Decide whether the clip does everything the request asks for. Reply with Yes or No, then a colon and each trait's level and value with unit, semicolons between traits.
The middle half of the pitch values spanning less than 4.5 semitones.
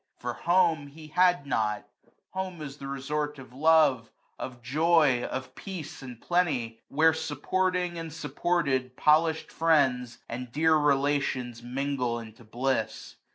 Yes: average, 4.1 semitones